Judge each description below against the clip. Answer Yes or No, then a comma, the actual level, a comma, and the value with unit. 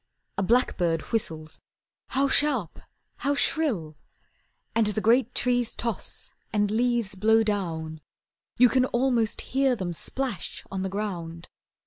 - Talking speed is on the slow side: Yes, slow, 125 wpm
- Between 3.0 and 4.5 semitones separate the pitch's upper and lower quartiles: No, average, 5.3 semitones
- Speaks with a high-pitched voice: Yes, high, 215 Hz